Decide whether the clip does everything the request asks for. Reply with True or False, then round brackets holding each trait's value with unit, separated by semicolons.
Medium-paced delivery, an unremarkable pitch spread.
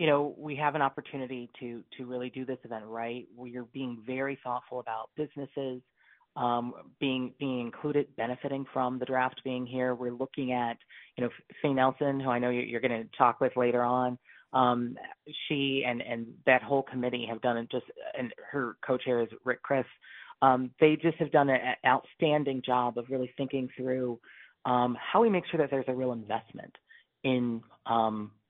False (185 wpm; 1.9 semitones)